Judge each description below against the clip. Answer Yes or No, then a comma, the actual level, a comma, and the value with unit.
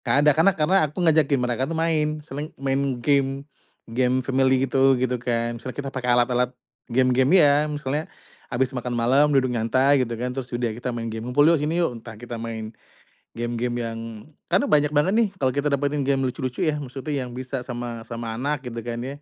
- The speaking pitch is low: Yes, low, 130 Hz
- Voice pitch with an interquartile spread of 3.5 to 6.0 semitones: No, average, 3.0 semitones